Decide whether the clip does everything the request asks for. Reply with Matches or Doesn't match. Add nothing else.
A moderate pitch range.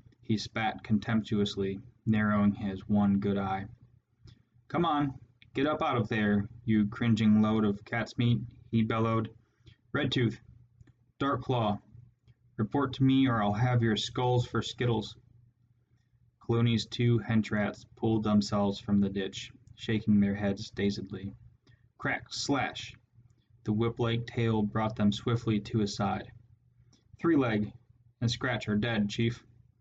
Doesn't match